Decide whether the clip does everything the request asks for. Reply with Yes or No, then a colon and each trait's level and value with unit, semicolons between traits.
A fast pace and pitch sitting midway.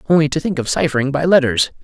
Yes: fast, 230 wpm; medium, 145 Hz